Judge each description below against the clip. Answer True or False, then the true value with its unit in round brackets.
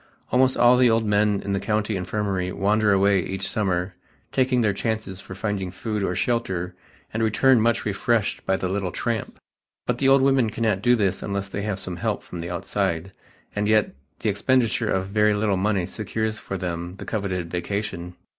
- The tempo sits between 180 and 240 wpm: True (195 wpm)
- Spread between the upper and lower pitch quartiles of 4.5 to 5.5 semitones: False (2.7 semitones)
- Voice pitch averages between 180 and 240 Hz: False (100 Hz)